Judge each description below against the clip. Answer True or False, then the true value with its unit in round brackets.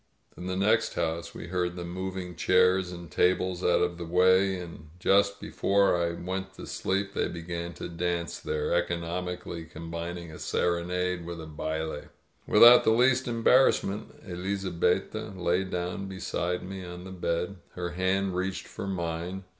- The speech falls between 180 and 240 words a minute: False (160 wpm)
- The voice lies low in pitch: True (90 Hz)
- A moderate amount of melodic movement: False (1.8 semitones)